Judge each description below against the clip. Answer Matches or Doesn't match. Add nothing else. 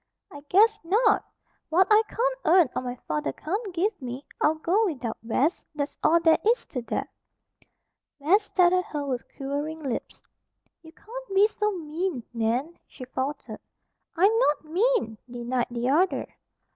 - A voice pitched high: Matches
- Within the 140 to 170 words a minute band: Matches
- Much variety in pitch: Matches